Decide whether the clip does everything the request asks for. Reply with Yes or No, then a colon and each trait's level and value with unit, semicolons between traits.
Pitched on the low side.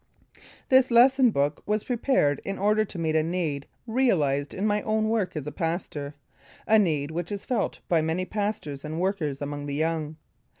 No: medium, 175 Hz